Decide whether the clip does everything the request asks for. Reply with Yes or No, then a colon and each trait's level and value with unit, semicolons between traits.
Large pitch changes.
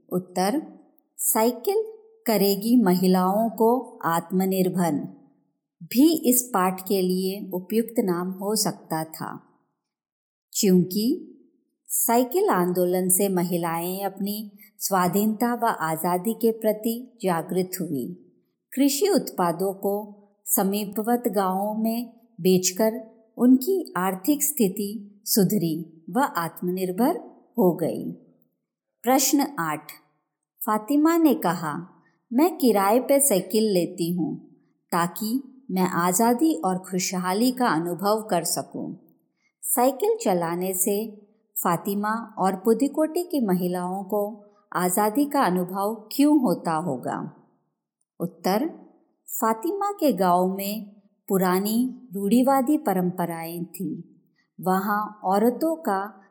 No: average, 4.9 semitones